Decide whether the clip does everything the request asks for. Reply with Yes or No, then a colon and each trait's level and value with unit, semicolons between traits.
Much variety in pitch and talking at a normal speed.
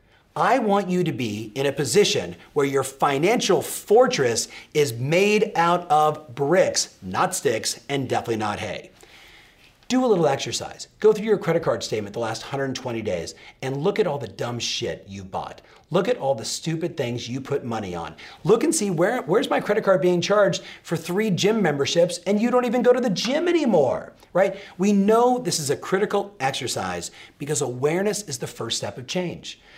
Yes: wide, 7.3 semitones; average, 190 wpm